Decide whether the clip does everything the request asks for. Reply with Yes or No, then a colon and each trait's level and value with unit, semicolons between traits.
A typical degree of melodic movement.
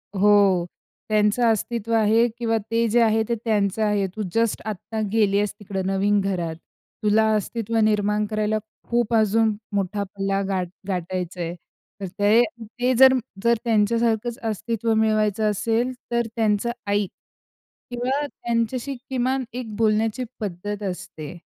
No: narrow, 2.3 semitones